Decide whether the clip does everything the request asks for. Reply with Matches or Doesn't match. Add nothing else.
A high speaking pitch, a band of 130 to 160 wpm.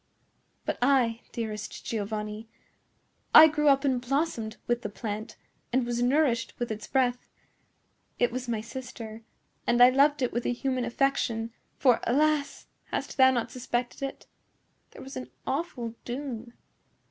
Matches